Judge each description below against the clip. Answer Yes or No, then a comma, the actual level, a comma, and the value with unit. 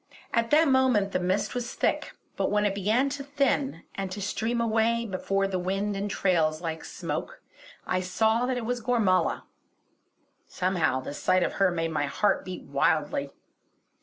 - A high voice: Yes, high, 200 Hz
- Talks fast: No, average, 170 wpm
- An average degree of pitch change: Yes, average, 4.2 semitones